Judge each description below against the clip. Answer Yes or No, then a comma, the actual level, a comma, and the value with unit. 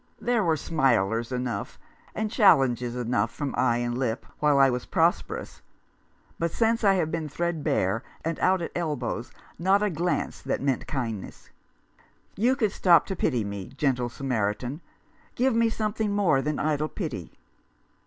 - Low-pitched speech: No, medium, 150 Hz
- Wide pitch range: Yes, wide, 7.6 semitones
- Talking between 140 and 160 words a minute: Yes, average, 155 wpm